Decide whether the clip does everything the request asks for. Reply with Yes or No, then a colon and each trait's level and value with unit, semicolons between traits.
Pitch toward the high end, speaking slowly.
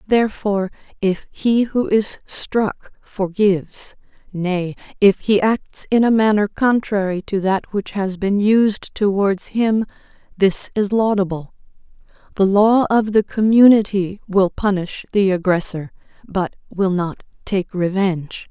Yes: high, 200 Hz; slow, 130 wpm